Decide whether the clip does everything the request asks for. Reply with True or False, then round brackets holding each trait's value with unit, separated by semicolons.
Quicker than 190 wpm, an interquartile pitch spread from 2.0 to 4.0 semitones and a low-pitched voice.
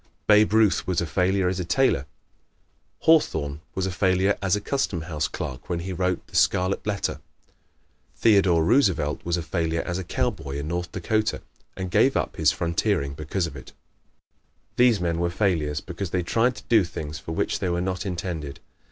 False (185 wpm; 3.3 semitones; 90 Hz)